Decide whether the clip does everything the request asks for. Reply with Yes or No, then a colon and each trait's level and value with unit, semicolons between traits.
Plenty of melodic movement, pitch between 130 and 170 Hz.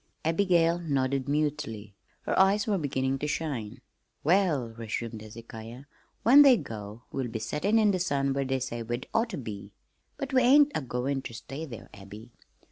Yes: wide, 7.0 semitones; low, 135 Hz